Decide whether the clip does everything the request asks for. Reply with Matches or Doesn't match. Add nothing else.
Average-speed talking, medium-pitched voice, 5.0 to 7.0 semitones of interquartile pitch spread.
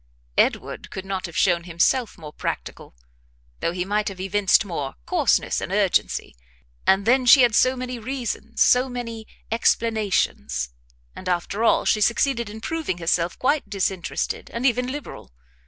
Doesn't match